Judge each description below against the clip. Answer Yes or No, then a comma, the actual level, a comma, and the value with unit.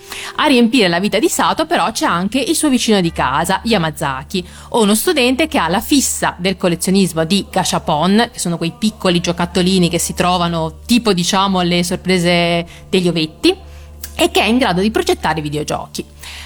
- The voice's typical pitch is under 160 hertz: No, medium, 185 Hz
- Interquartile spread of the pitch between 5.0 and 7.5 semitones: Yes, wide, 5.5 semitones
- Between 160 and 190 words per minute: Yes, fast, 170 wpm